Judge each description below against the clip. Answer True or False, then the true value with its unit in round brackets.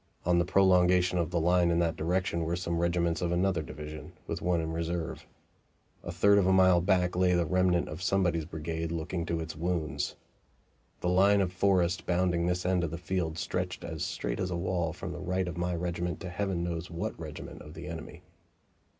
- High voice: False (85 Hz)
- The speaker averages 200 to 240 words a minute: True (205 wpm)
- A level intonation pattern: True (1.5 semitones)